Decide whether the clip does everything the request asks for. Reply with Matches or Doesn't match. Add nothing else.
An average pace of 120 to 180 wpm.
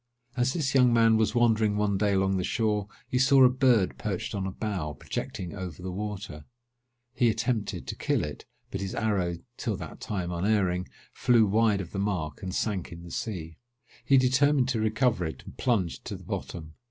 Doesn't match